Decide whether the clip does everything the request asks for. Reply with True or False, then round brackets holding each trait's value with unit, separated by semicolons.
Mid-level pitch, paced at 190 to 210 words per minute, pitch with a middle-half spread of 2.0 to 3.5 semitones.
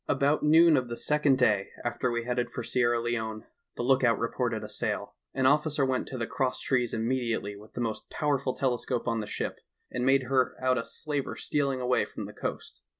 False (125 Hz; 205 wpm; 2.5 semitones)